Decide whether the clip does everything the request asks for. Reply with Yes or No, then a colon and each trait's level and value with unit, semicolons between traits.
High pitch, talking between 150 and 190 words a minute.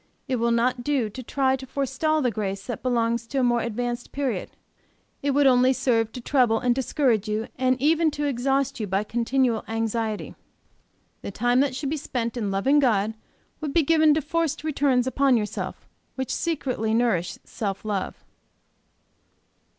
Yes: very high, 250 Hz; average, 170 wpm